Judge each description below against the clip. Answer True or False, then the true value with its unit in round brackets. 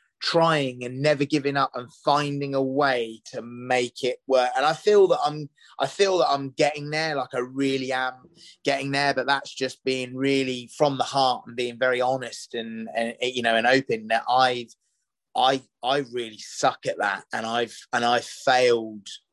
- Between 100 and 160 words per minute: False (190 wpm)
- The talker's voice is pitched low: True (130 Hz)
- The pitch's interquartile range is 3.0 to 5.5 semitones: False (2.5 semitones)